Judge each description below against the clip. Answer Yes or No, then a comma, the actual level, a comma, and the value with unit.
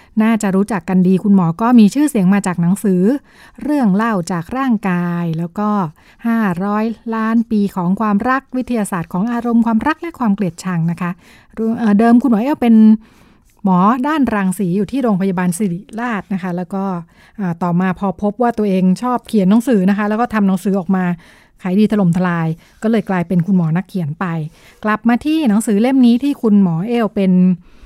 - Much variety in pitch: No, average, 3.7 semitones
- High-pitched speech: Yes, high, 205 Hz